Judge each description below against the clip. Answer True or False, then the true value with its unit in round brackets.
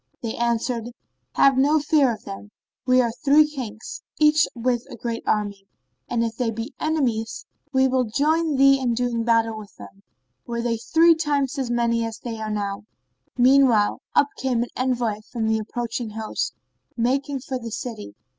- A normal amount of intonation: True (3.3 semitones)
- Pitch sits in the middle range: False (240 Hz)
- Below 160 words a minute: False (175 wpm)